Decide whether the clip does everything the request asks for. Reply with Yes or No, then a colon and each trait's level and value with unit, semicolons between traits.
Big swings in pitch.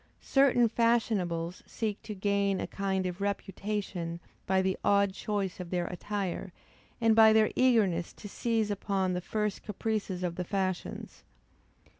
No: average, 2.8 semitones